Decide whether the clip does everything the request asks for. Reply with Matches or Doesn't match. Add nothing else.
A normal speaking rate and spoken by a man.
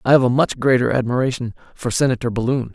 Matches